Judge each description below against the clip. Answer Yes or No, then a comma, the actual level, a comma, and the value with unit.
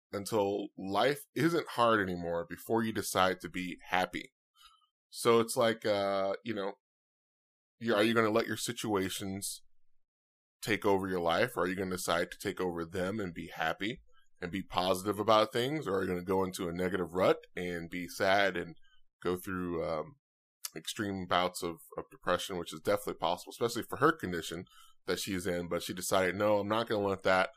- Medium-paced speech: Yes, average, 195 wpm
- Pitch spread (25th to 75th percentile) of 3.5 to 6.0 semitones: No, average, 2.8 semitones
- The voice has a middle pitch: No, very low, 95 Hz